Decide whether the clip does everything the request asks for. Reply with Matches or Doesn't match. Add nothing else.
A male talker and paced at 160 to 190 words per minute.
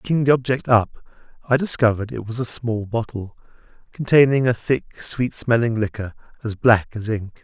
Matches